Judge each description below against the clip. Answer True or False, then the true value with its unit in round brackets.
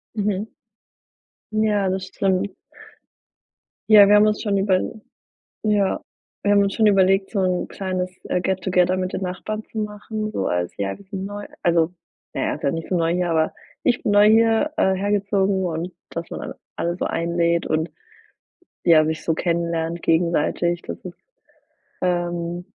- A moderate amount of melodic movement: True (3.1 semitones)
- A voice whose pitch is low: False (185 Hz)